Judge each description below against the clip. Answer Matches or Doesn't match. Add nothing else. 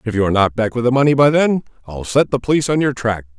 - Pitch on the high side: Doesn't match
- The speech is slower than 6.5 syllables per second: Doesn't match